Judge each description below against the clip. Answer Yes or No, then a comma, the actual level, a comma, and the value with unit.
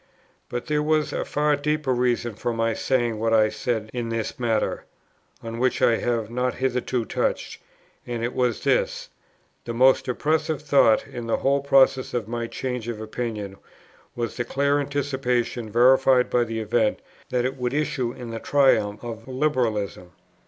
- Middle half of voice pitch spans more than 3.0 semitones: No, narrow, 2.6 semitones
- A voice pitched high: No, low, 120 Hz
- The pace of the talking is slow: No, average, 165 wpm